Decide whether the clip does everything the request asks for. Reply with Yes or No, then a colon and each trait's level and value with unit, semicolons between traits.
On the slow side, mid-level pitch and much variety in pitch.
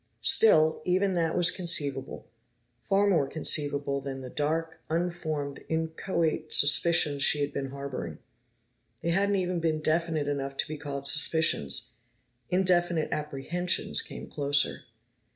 No: slow, 125 wpm; medium, 155 Hz; average, 3.3 semitones